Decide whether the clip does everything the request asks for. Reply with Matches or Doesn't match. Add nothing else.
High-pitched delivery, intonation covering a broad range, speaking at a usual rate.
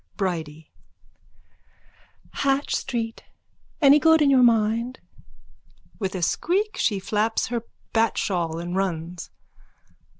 Doesn't match